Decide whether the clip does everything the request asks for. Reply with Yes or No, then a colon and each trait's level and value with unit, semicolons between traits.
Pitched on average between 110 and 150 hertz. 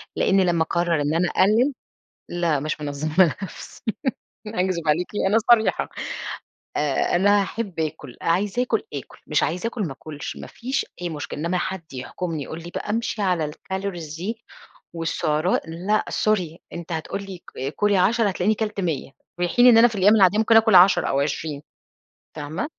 No: medium, 180 Hz